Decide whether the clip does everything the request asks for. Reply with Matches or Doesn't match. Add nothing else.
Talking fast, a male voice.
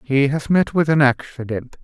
Doesn't match